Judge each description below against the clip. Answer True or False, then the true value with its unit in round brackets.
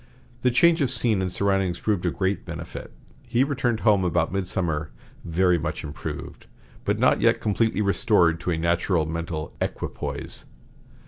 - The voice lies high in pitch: False (95 Hz)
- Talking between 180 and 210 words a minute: False (150 wpm)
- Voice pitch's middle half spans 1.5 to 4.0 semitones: False (4.5 semitones)